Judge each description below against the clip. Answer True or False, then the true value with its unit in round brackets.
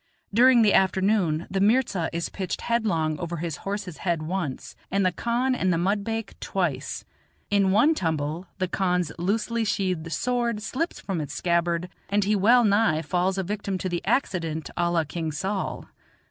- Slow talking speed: False (170 wpm)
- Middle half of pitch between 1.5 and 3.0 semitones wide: False (3.8 semitones)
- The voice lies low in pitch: False (190 Hz)